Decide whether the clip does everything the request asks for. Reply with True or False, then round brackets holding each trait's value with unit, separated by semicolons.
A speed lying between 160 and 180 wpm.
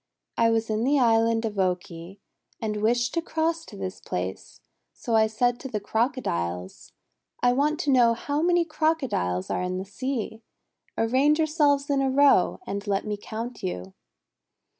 True (165 wpm)